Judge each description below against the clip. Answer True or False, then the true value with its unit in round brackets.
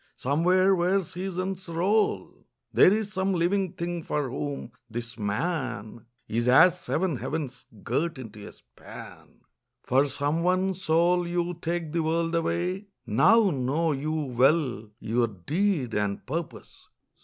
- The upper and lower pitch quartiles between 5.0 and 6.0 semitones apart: True (5.6 semitones)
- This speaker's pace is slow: True (130 wpm)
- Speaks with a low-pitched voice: False (165 Hz)